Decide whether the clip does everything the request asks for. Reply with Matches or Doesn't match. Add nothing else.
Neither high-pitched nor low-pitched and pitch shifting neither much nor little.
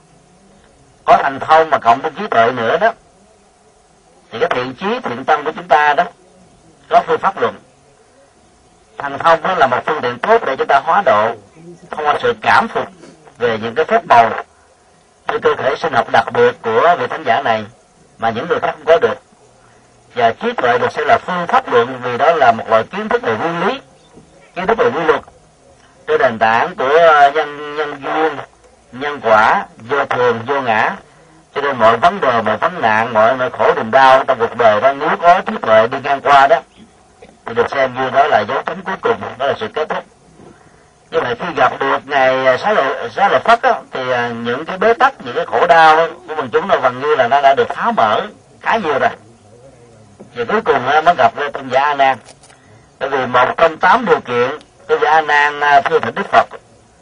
Doesn't match